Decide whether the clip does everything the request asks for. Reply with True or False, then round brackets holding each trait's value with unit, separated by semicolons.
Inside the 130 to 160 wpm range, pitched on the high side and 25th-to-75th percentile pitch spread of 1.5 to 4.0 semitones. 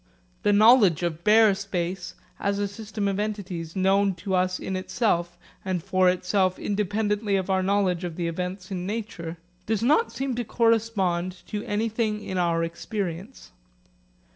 True (155 wpm; 195 Hz; 2.7 semitones)